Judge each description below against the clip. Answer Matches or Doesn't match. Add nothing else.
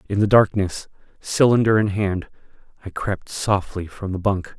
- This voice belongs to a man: Matches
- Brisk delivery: Doesn't match